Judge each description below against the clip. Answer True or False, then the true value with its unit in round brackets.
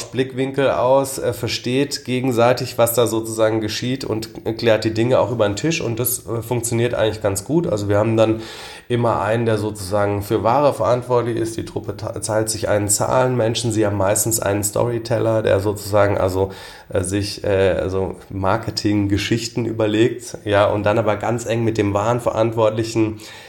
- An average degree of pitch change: False (2.2 semitones)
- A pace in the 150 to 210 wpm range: True (170 wpm)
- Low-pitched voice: True (110 Hz)